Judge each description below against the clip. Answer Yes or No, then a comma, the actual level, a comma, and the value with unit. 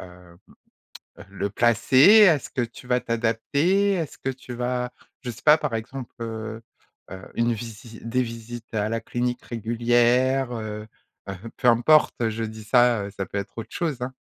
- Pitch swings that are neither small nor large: No, narrow, 2.3 semitones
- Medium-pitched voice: No, low, 120 Hz